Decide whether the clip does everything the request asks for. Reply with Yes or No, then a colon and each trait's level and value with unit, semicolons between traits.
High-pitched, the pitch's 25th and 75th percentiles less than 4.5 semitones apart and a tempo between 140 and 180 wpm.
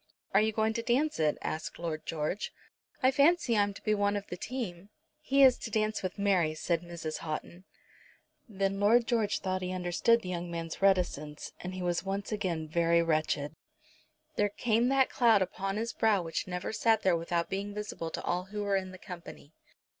No: high, 195 Hz; average, 4.1 semitones; average, 200 wpm